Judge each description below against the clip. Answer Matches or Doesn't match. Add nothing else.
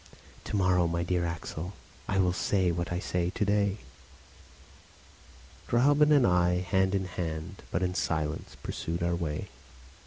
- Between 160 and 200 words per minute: Doesn't match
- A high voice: Doesn't match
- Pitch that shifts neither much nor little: Doesn't match